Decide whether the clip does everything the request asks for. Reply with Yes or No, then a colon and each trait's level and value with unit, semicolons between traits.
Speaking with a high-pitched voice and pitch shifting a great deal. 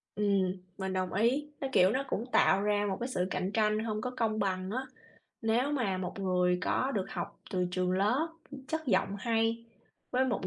No: high, 210 Hz; average, 3.9 semitones